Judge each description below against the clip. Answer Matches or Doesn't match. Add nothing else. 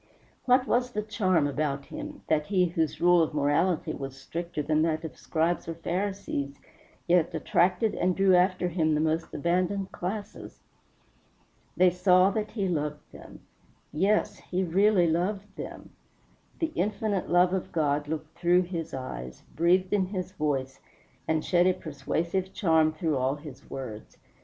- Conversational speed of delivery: Matches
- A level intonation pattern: Doesn't match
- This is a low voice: Doesn't match